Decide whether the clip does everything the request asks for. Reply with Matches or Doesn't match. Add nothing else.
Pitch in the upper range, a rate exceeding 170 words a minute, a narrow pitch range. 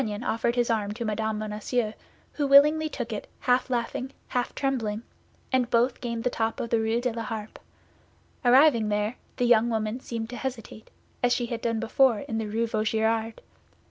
Matches